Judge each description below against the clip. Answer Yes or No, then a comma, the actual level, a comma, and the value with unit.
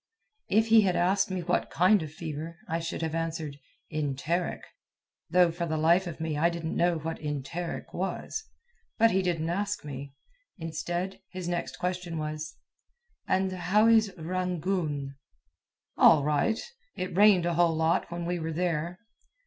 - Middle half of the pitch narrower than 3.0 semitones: Yes, narrow, 2.5 semitones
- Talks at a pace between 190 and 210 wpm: No, average, 155 wpm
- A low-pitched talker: No, medium, 170 Hz